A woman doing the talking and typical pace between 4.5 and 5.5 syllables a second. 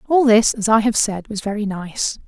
Yes: female; 5.0 syllables/s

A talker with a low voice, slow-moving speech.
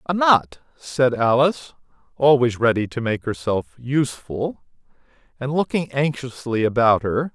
Yes: low, 130 Hz; slow, 120 wpm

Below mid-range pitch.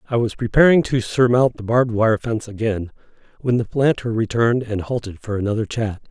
Yes: low, 115 Hz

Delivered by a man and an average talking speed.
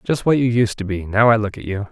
No: male; fast, 345 wpm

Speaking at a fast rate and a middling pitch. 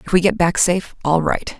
Yes: fast, 225 wpm; medium, 175 Hz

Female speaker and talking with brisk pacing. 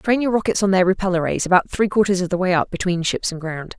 Yes: female; fast, 285 wpm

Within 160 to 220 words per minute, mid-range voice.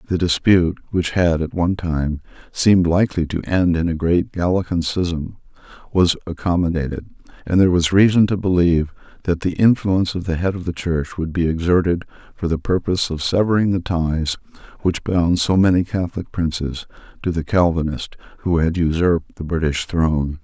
No: average, 170 wpm; very low, 85 Hz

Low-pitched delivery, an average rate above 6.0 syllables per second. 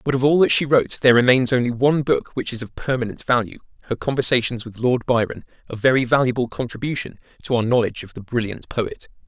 Yes: low, 125 Hz; 6.4 syllables/s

